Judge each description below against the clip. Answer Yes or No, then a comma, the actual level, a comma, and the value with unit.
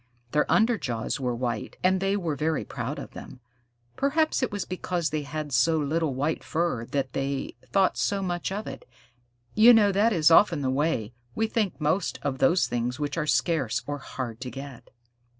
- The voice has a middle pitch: Yes, medium, 155 Hz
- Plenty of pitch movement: Yes, wide, 5.9 semitones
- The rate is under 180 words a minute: No, average, 190 wpm